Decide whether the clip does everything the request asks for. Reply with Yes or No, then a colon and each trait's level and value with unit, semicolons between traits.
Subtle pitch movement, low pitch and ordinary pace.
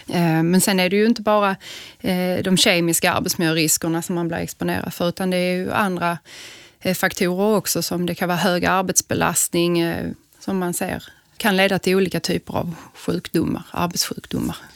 No: narrow, 1.8 semitones; medium, 180 Hz; average, 165 wpm